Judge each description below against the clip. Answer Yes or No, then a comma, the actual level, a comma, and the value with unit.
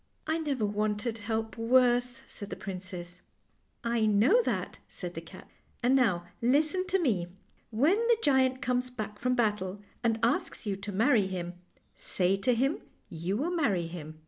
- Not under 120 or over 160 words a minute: No, average, 180 wpm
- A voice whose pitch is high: Yes, high, 225 Hz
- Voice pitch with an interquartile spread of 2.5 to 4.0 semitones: No, average, 4.8 semitones